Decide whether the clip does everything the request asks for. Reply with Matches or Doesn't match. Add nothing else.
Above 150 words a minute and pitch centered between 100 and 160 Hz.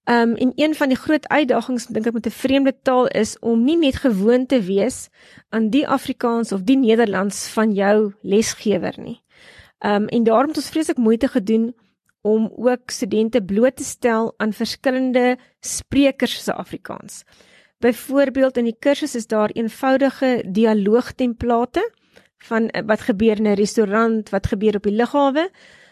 Doesn't match